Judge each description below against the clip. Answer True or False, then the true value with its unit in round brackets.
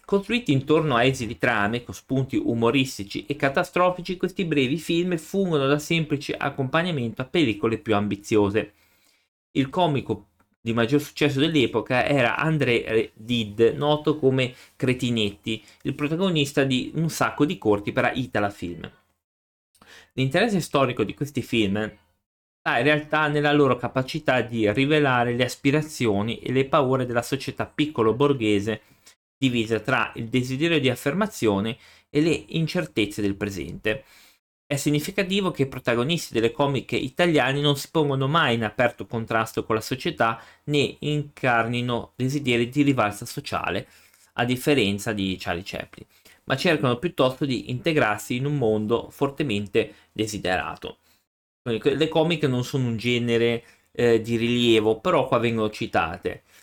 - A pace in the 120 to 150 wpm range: True (135 wpm)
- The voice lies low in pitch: True (130 Hz)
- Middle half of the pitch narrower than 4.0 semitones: False (4.7 semitones)